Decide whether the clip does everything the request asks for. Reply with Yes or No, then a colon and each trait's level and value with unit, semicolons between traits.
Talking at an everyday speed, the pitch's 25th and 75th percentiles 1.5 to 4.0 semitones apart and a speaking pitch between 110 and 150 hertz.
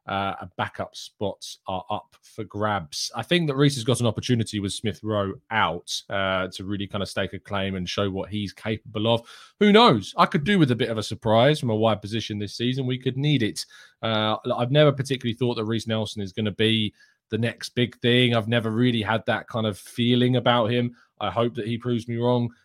No: fast, 235 wpm; average, 2.7 semitones; low, 115 Hz